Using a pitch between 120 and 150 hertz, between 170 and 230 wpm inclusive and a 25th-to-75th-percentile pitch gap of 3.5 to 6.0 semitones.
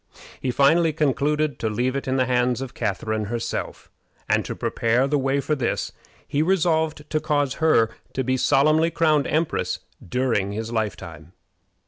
No: low, 135 Hz; average, 160 wpm; average, 4.6 semitones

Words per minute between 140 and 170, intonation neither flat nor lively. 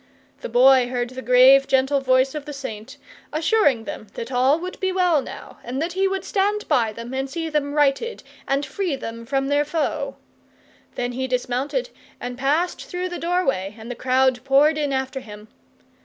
No: average, 185 wpm; average, 3.8 semitones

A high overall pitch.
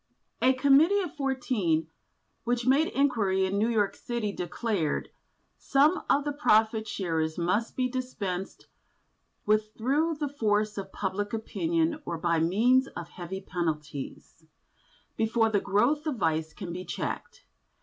Yes: high, 215 Hz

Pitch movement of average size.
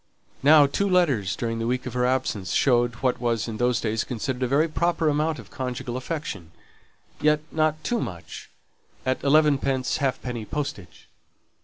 Yes: average, 4.1 semitones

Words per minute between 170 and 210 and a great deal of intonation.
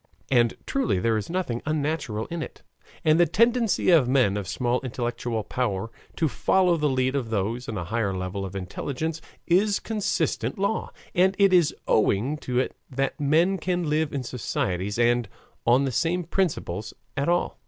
Yes: average, 175 wpm; wide, 6.9 semitones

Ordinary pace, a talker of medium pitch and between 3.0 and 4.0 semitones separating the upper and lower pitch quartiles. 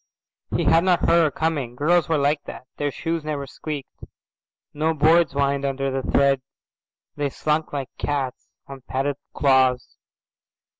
No: average, 150 wpm; medium, 145 Hz; narrow, 2.5 semitones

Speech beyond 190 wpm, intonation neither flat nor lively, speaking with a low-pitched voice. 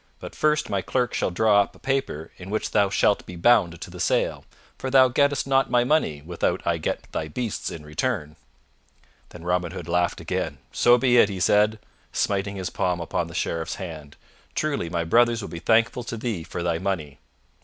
No: average, 200 wpm; wide, 6.1 semitones; low, 100 Hz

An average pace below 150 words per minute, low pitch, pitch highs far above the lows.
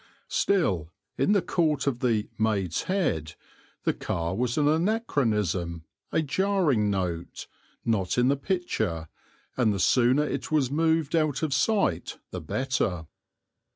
Yes: slow, 135 wpm; low, 130 Hz; wide, 8.8 semitones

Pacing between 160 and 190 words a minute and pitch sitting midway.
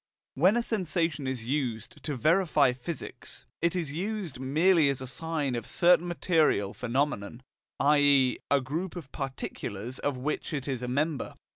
Yes: average, 165 wpm; medium, 145 Hz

